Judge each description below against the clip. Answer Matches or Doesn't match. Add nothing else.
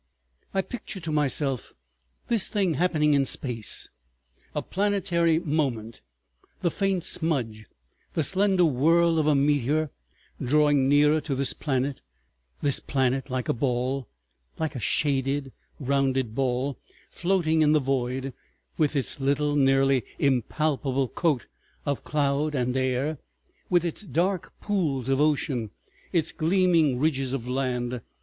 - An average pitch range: Matches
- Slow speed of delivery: Matches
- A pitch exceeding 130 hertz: Matches